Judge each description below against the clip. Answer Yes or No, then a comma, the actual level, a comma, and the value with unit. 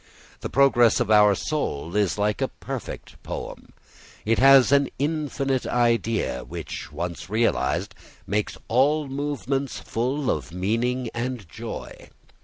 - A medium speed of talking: No, slow, 125 wpm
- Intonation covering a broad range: No, average, 4.6 semitones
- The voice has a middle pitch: No, low, 120 Hz